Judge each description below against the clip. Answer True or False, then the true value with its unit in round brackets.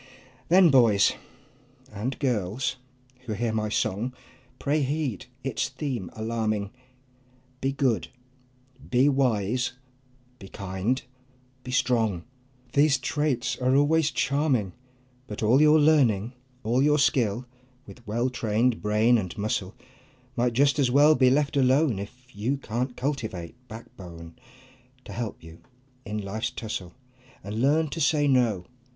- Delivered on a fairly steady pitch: False (4.5 semitones)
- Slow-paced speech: True (130 wpm)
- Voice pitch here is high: False (125 Hz)